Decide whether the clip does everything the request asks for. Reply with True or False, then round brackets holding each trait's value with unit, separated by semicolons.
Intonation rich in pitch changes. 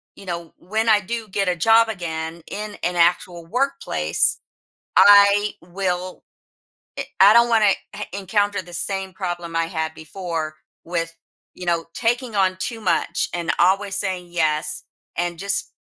False (3.2 semitones)